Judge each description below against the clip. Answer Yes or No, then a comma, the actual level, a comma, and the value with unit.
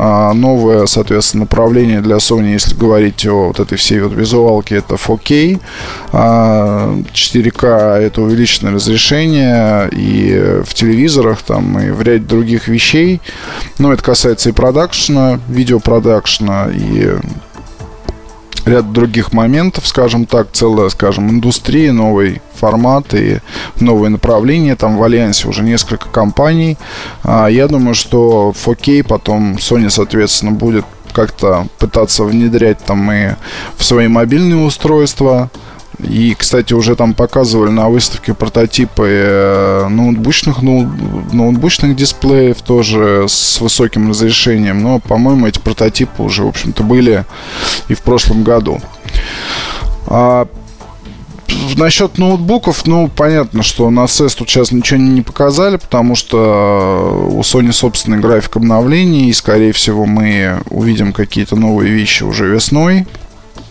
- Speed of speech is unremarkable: Yes, average, 120 wpm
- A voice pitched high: No, low, 115 Hz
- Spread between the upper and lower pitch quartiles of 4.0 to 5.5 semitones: No, average, 2.9 semitones